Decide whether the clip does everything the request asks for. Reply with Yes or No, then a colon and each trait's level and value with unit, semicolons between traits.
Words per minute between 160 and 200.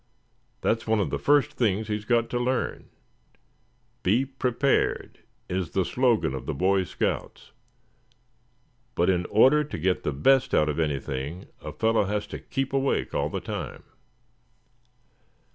No: average, 145 wpm